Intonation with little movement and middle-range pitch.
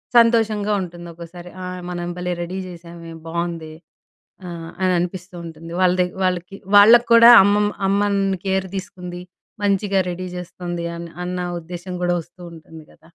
Yes: narrow, 2.1 semitones; medium, 180 Hz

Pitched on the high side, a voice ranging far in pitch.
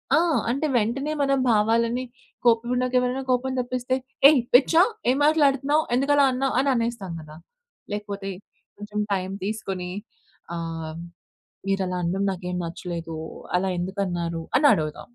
Yes: high, 220 Hz; wide, 6.3 semitones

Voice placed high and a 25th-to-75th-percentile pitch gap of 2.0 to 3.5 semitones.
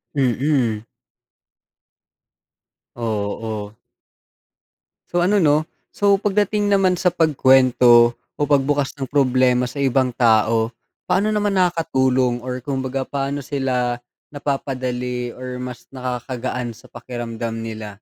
No: low, 130 Hz; average, 3.2 semitones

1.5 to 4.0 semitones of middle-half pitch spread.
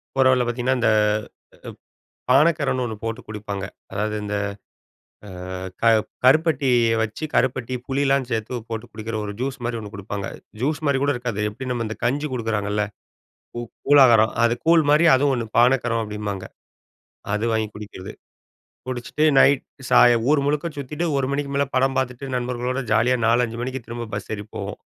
Yes: average, 3.4 semitones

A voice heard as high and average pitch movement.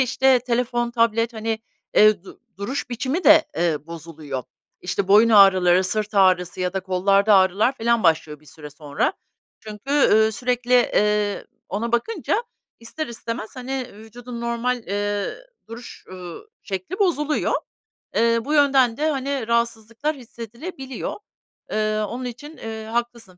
Yes: high, 230 Hz; average, 4.0 semitones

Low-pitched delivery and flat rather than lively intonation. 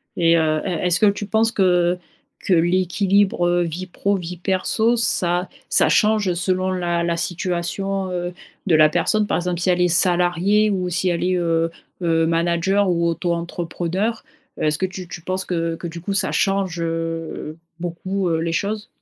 No: medium, 175 Hz; narrow, 2.2 semitones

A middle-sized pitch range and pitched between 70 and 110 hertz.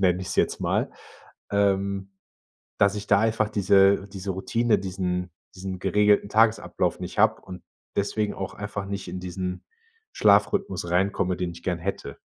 No: narrow, 1.8 semitones; low, 100 Hz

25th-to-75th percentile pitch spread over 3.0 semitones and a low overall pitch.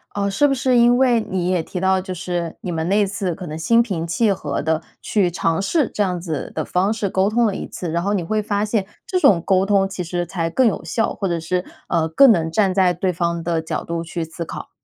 No: average, 3.5 semitones; medium, 185 Hz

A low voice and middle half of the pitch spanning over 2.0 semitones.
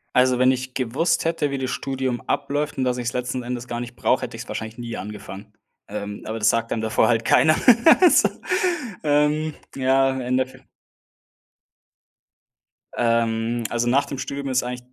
Yes: low, 125 Hz; narrow, 2.6 semitones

